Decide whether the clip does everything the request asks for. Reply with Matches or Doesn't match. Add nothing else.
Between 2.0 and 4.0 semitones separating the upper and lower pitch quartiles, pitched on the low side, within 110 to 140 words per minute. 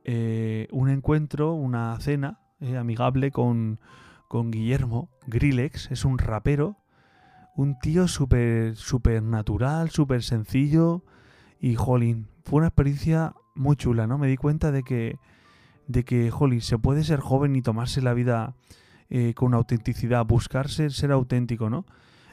Matches